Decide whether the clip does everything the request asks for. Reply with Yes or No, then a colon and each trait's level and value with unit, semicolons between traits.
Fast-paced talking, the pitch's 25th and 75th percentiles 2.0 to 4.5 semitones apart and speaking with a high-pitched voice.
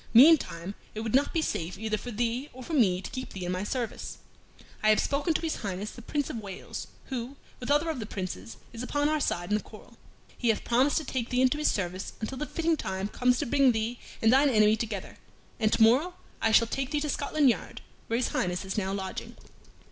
No: fast, 235 wpm; average, 5.2 semitones; high, 235 Hz